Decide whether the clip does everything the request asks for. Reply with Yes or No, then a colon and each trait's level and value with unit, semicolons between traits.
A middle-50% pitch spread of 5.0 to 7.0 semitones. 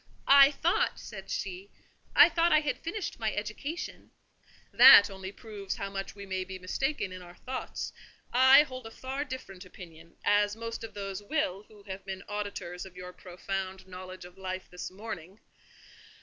Yes: wide, 5.5 semitones